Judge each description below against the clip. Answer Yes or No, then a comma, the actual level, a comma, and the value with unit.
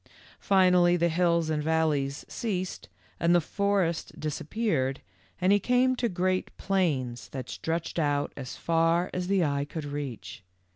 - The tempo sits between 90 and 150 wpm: Yes, average, 140 wpm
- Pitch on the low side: No, medium, 170 Hz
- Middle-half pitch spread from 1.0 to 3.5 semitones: No, average, 4.1 semitones